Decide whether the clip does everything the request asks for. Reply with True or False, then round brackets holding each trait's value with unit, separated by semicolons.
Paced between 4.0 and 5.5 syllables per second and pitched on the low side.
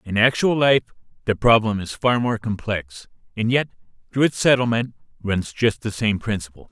True (5.0 syllables/s; 110 Hz)